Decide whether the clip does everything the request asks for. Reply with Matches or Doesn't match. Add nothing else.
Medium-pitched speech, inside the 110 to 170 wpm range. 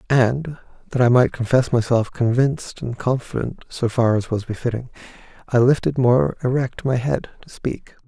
Doesn't match